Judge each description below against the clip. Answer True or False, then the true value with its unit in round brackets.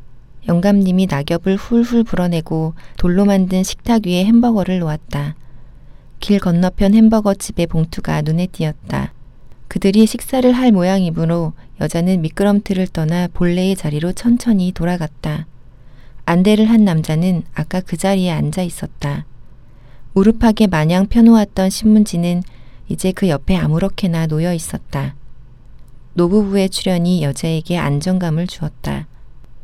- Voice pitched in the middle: True (175 Hz)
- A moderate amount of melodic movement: True (4.4 semitones)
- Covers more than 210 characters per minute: True (295 characters per minute)